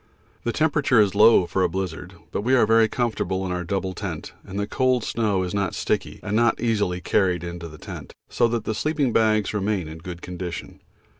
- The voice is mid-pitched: No, low, 100 Hz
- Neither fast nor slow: No, fast, 210 wpm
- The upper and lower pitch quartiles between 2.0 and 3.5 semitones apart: No, average, 4.0 semitones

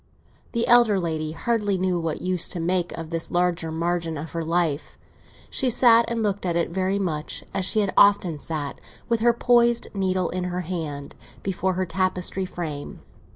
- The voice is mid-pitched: Yes, medium, 180 Hz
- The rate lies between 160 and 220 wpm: Yes, average, 180 wpm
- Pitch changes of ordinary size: Yes, average, 3.4 semitones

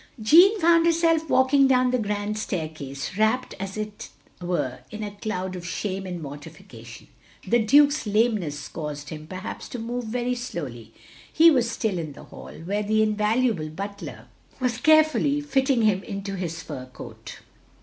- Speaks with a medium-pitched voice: No, high, 210 Hz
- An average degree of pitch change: No, wide, 7.0 semitones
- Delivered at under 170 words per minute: Yes, average, 160 wpm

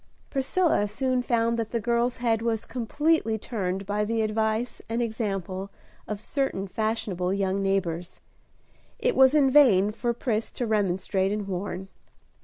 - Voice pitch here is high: Yes, high, 220 Hz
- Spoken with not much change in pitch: No, average, 3.5 semitones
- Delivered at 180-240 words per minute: No, average, 145 wpm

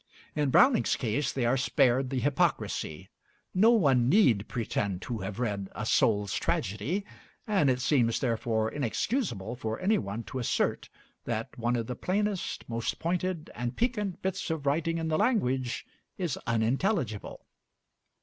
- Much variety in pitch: Yes, wide, 7.4 semitones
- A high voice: No, low, 130 Hz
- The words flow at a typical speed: Yes, average, 150 wpm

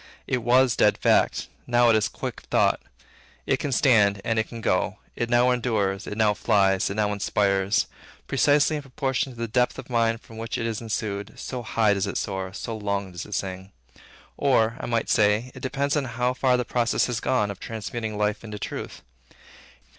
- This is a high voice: No, low, 115 Hz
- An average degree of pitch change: Yes, average, 3.1 semitones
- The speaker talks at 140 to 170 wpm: No, average, 195 wpm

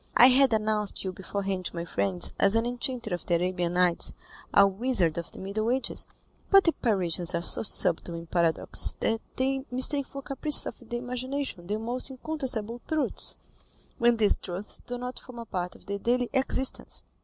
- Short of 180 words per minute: No, average, 185 wpm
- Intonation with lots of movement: Yes, wide, 5.7 semitones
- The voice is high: Yes, high, 225 Hz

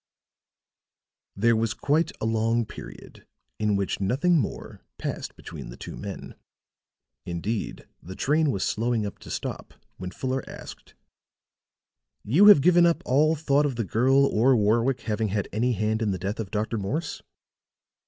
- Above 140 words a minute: Yes, average, 155 wpm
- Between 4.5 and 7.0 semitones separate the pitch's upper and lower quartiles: Yes, average, 4.9 semitones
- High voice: No, low, 115 Hz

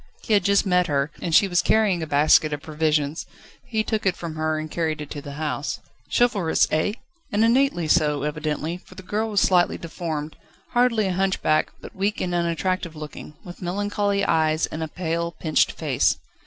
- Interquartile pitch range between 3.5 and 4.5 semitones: Yes, average, 4.2 semitones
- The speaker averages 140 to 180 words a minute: No, average, 190 wpm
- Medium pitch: Yes, medium, 170 Hz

